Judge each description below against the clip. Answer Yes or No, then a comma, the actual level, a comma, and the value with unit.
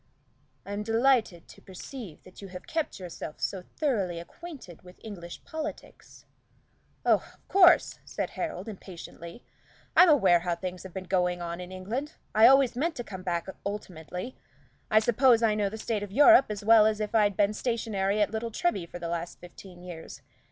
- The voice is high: Yes, high, 205 Hz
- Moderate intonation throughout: Yes, average, 4.5 semitones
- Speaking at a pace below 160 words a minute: No, average, 180 wpm